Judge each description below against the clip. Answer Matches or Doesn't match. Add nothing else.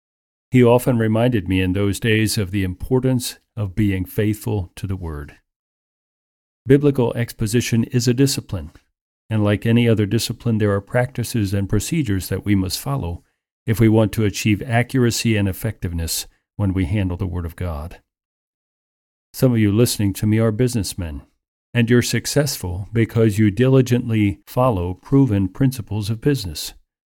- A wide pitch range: Doesn't match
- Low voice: Matches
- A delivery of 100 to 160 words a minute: Matches